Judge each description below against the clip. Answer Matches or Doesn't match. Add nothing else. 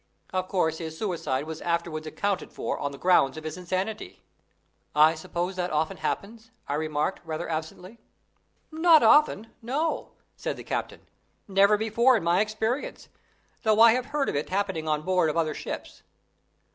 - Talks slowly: Doesn't match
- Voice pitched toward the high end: Doesn't match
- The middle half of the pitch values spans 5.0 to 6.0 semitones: Matches